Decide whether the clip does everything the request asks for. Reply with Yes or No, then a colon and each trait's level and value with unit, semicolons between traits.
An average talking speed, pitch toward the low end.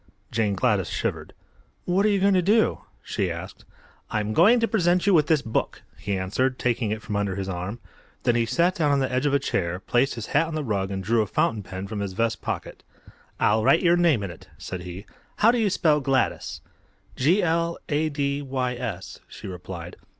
No: fast, 215 wpm; low, 125 Hz